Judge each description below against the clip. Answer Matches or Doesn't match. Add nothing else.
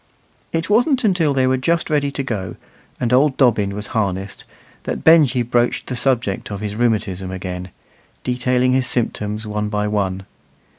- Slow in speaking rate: Doesn't match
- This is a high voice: Doesn't match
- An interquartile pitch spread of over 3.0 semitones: Matches